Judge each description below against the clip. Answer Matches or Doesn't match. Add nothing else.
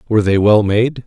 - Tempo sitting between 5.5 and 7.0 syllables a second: Matches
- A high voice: Doesn't match